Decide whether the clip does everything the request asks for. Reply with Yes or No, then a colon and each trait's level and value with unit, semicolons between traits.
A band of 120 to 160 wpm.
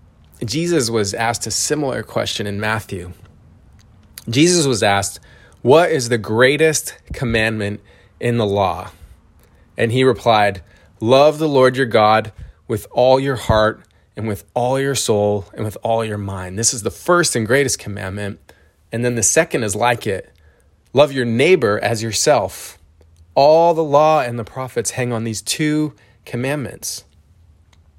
Yes: average, 150 wpm